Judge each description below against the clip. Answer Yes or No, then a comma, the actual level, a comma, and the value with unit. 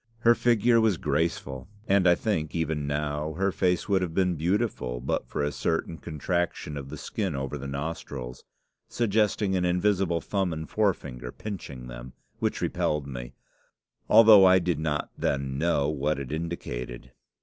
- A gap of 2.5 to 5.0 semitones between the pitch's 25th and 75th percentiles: No, wide, 5.4 semitones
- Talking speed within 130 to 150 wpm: No, average, 160 wpm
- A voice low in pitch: Yes, very low, 80 Hz